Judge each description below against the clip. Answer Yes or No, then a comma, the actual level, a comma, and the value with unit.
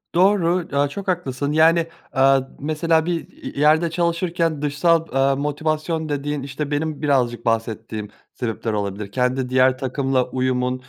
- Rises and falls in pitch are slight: No, average, 4.0 semitones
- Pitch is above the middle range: No, medium, 145 Hz